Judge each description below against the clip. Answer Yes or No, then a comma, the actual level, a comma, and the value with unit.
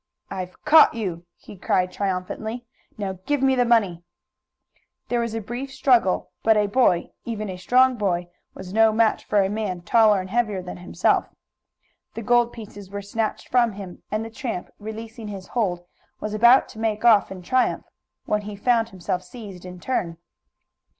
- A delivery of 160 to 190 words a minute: Yes, average, 175 wpm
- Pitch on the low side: No, high, 215 Hz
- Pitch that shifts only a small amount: No, average, 3.8 semitones